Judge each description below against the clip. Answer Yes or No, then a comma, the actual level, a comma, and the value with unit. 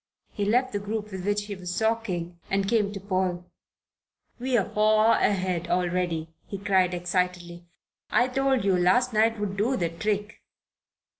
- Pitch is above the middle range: Yes, high, 200 Hz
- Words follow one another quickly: No, average, 155 wpm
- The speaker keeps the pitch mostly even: No, average, 3.1 semitones